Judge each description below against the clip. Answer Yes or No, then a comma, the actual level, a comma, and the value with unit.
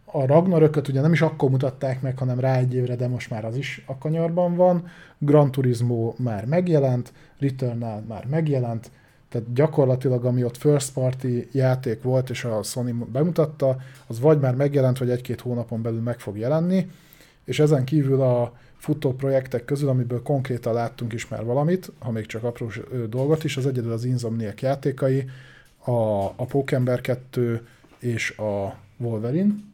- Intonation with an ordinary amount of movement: Yes, average, 3.2 semitones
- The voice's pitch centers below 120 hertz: No, low, 130 Hz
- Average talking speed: No, fast, 165 wpm